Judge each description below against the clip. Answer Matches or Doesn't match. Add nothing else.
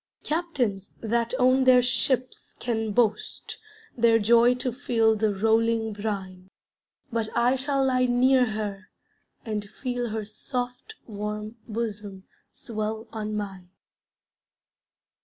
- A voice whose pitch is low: Doesn't match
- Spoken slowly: Matches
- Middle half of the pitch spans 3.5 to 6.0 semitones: Doesn't match